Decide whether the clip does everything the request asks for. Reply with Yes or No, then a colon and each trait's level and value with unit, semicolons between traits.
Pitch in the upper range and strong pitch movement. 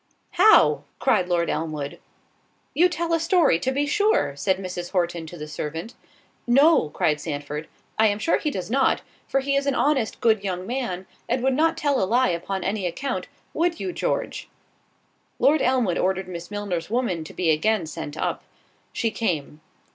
Yes: high, 205 Hz; wide, 8.2 semitones